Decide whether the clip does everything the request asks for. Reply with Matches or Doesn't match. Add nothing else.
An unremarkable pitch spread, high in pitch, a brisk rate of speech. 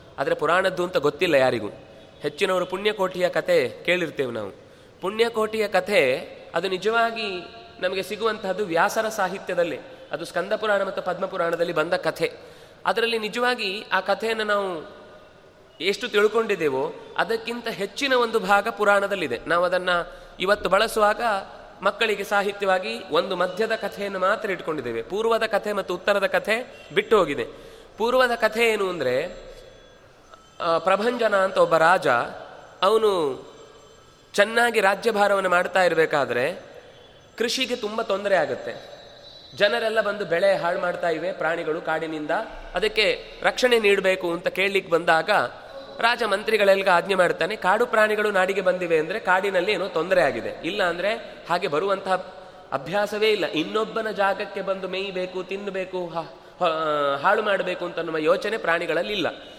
Matches